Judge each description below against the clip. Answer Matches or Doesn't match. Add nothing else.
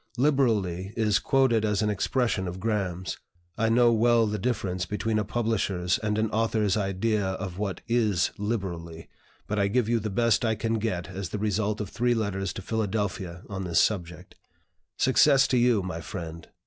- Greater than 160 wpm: Matches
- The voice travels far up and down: Doesn't match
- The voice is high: Doesn't match